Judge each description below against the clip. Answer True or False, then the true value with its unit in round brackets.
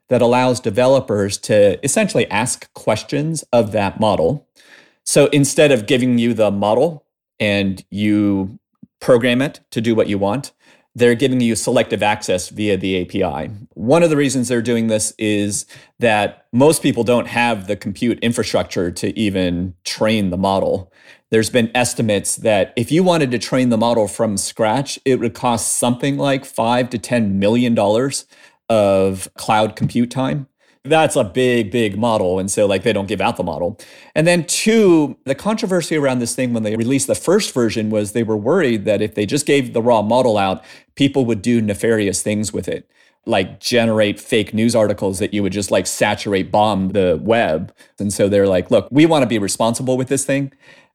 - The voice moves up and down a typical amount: True (4.1 semitones)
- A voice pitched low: True (115 Hz)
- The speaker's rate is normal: True (185 wpm)